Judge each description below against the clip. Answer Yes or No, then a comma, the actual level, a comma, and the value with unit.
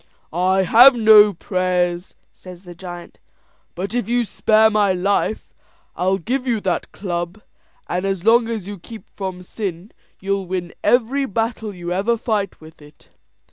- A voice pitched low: No, high, 195 Hz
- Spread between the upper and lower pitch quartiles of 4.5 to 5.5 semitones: No, average, 3.6 semitones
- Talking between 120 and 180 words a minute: Yes, average, 155 wpm